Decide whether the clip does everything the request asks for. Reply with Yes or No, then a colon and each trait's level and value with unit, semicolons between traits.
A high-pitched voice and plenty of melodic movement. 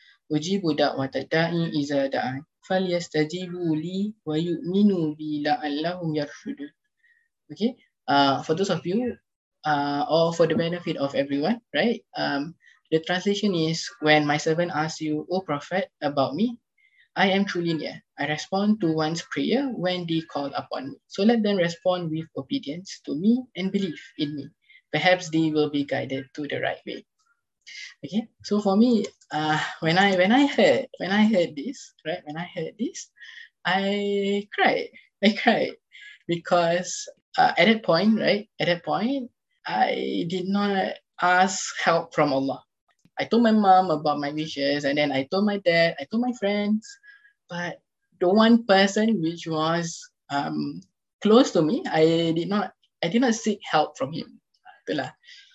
No: medium, 180 Hz; wide, 6.2 semitones